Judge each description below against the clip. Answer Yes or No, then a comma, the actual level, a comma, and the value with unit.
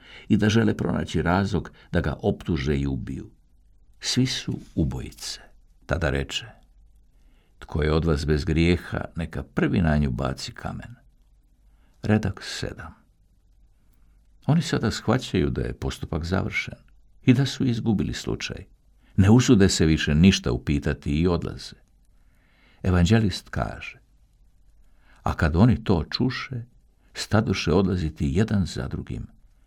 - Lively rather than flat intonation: Yes, wide, 5.7 semitones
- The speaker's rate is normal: Yes, average, 125 wpm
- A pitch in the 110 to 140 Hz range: No, very low, 90 Hz